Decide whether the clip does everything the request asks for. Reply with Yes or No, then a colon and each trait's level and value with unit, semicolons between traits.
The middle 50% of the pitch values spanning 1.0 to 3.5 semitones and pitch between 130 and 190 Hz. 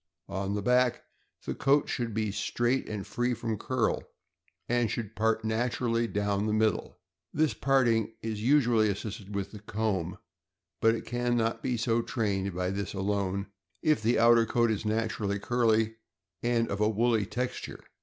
No: narrow, 2.6 semitones; low, 110 Hz